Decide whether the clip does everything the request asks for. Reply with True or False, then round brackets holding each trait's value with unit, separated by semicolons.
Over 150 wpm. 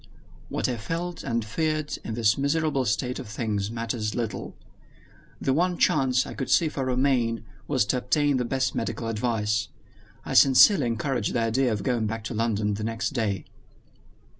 True (170 wpm)